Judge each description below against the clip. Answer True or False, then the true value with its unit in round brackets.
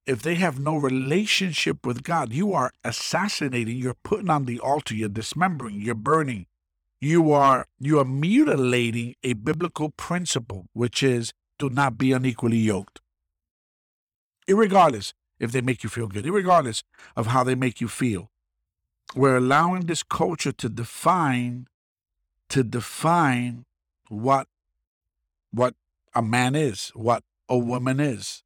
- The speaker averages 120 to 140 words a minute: True (135 wpm)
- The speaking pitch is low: True (125 Hz)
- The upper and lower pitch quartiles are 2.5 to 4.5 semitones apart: False (5.3 semitones)